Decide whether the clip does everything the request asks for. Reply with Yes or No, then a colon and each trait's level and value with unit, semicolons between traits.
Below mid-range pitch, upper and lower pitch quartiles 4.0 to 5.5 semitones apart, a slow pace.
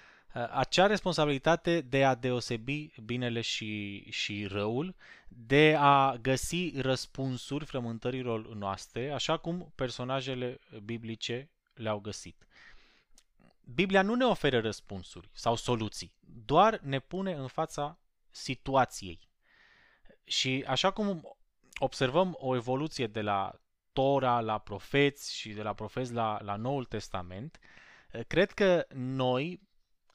Yes: low, 130 Hz; average, 4.8 semitones; slow, 110 wpm